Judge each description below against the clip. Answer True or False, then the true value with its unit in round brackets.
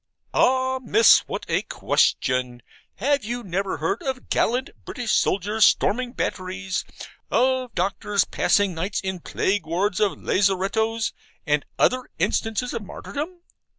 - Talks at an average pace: False (125 wpm)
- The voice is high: True (205 Hz)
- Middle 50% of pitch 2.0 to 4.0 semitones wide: False (4.9 semitones)